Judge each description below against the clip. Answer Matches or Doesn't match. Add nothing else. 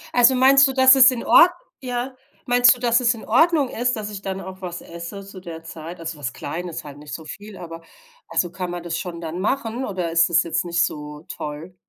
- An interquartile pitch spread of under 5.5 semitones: Doesn't match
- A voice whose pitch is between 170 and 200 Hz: Matches